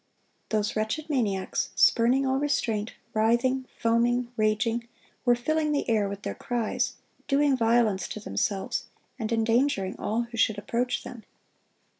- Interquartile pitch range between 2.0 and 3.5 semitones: Yes, average, 2.7 semitones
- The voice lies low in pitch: No, high, 230 Hz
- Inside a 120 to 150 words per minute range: Yes, slow, 135 wpm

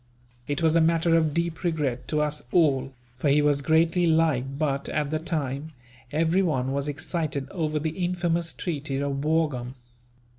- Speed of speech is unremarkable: Yes, average, 160 wpm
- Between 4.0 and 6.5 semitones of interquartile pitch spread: No, narrow, 2.6 semitones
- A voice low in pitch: No, medium, 155 Hz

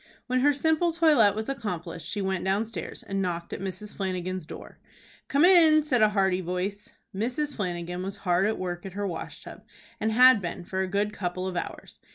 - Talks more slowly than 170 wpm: No, average, 200 wpm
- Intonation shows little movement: No, average, 4.6 semitones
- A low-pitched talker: No, high, 195 Hz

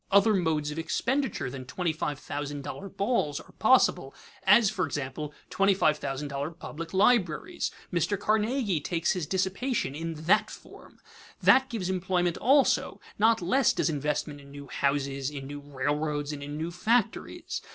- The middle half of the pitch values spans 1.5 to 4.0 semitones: No, wide, 5.6 semitones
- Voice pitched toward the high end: No, medium, 165 Hz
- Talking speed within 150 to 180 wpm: Yes, average, 160 wpm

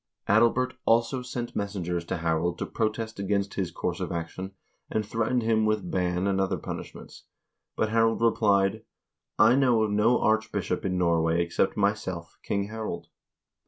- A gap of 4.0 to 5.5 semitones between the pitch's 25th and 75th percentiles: No, average, 3.5 semitones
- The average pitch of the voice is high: No, low, 105 Hz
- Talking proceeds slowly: No, average, 160 wpm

